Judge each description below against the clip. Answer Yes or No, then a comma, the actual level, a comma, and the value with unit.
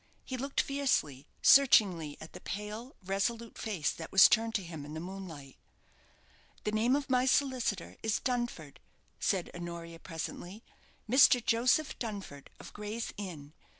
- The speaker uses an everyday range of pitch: No, wide, 6.2 semitones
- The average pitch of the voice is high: Yes, high, 205 Hz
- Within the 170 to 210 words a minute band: No, average, 145 wpm